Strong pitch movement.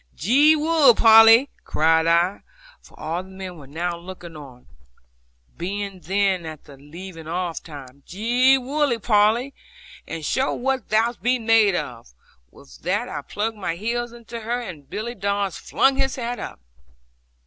Yes: wide, 6.1 semitones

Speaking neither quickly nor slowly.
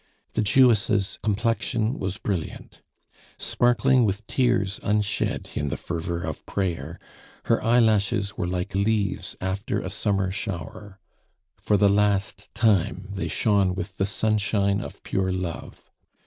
No: slow, 130 wpm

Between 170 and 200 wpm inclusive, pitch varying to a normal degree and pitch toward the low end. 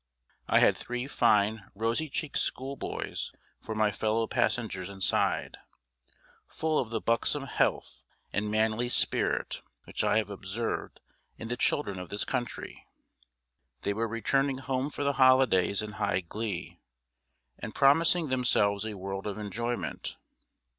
No: slow, 135 wpm; average, 4.1 semitones; low, 115 Hz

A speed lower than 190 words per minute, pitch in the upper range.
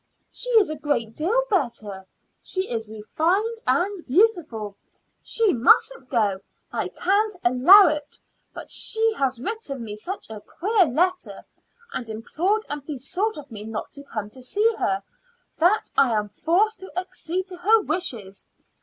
Yes: average, 155 wpm; very high, 310 Hz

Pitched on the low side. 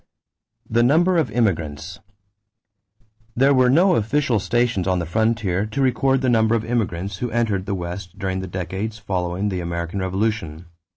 Yes: low, 105 Hz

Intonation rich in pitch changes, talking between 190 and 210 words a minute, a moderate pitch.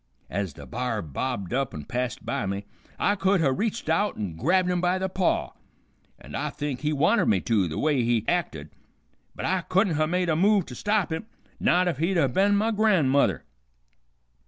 Yes: wide, 7.7 semitones; average, 200 wpm; medium, 160 Hz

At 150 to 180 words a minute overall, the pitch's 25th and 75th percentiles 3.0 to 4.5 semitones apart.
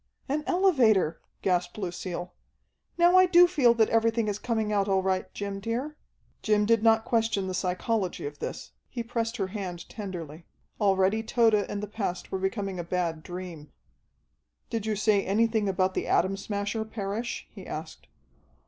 Yes: average, 165 wpm; average, 3.4 semitones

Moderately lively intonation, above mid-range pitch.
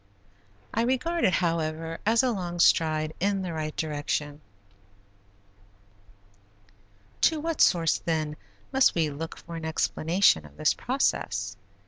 No: average, 4.1 semitones; medium, 165 Hz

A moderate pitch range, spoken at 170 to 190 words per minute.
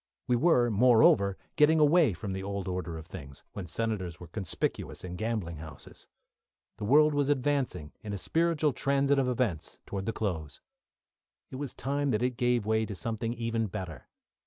No: wide, 6.3 semitones; average, 175 wpm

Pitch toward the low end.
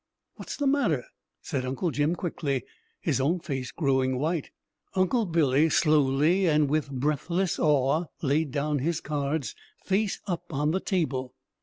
No: medium, 150 Hz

